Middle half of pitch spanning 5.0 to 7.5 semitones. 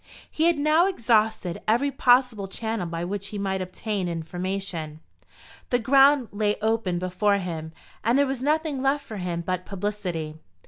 Yes: wide, 5.6 semitones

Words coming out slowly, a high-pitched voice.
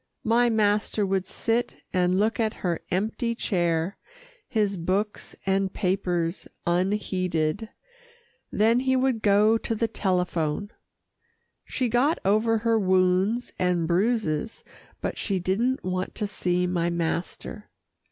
Yes: slow, 125 wpm; high, 200 Hz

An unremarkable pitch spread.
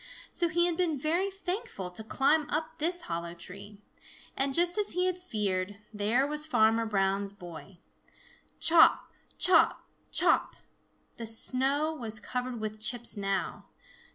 No: wide, 8.0 semitones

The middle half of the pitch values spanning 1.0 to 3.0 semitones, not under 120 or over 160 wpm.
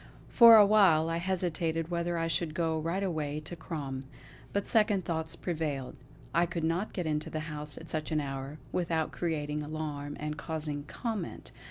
No: narrow, 2.4 semitones; average, 175 wpm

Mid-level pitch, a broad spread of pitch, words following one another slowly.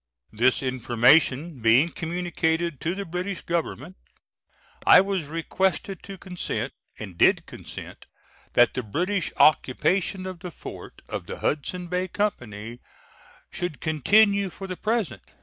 Yes: medium, 170 Hz; wide, 6.2 semitones; slow, 130 wpm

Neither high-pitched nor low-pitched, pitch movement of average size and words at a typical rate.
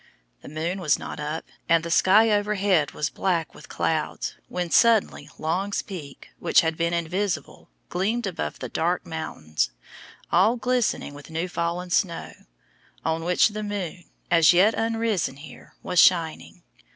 Yes: medium, 175 Hz; average, 4.0 semitones; average, 150 wpm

